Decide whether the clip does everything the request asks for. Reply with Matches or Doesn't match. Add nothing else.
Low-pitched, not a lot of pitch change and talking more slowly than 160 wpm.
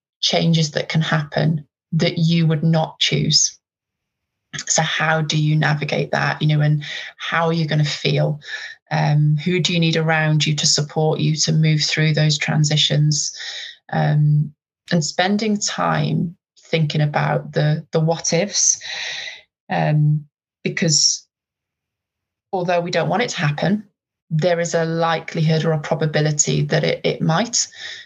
Doesn't match